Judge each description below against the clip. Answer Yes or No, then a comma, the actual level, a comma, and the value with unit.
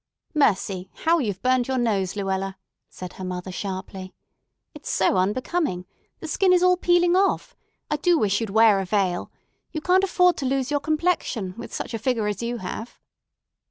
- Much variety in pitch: Yes, wide, 8.6 semitones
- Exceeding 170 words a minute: Yes, average, 180 wpm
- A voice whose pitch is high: Yes, high, 230 Hz